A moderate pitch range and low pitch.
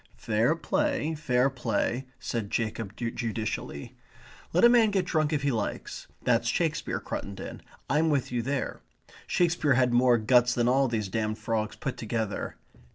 Yes: average, 4.7 semitones; low, 125 Hz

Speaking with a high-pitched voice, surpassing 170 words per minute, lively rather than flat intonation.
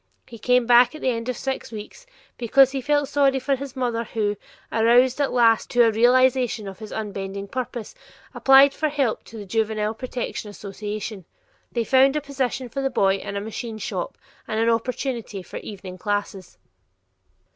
No: high, 235 Hz; average, 180 wpm; average, 3.6 semitones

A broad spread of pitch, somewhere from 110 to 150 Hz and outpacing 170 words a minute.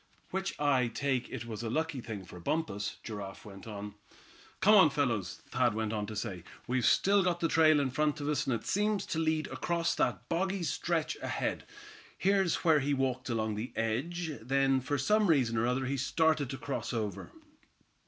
Yes: wide, 6.3 semitones; low, 135 Hz; average, 195 wpm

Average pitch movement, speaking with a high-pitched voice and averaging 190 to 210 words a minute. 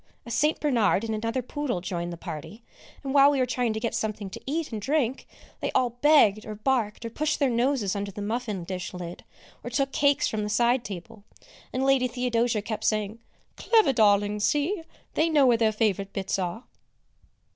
Yes: average, 4.4 semitones; high, 230 Hz; average, 195 wpm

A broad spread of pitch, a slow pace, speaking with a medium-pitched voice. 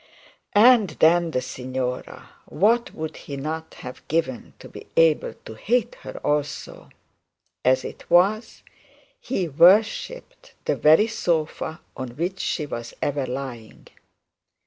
Yes: wide, 6.7 semitones; slow, 125 wpm; medium, 160 Hz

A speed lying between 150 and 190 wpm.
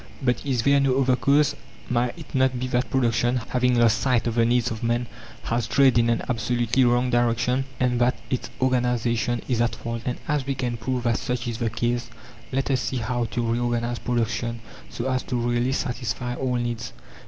No: average, 200 wpm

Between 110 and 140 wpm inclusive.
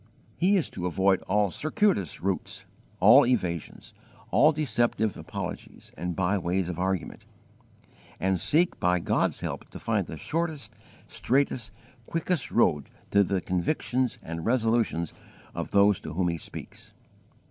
Yes: slow, 135 wpm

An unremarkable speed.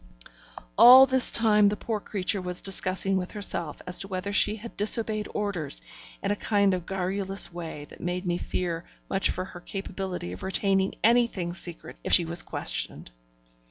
Yes: average, 170 wpm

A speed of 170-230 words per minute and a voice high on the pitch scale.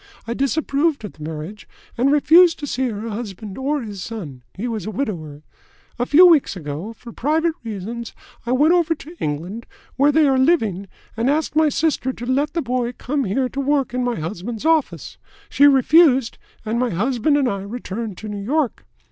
Yes: average, 190 wpm; high, 245 Hz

